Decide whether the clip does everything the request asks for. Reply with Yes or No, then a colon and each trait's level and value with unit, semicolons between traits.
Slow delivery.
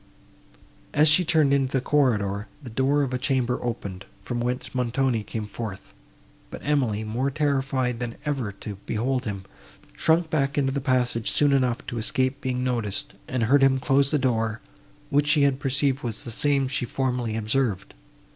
No: average, 175 wpm